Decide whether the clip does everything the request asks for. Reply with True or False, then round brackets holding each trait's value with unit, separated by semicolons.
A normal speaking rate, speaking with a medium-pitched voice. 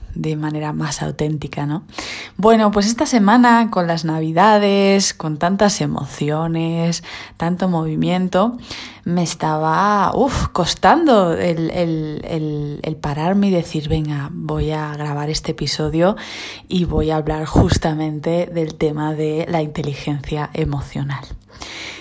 False (120 wpm; 160 Hz)